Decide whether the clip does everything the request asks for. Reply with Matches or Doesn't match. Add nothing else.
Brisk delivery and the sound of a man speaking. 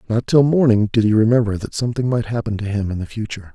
Matches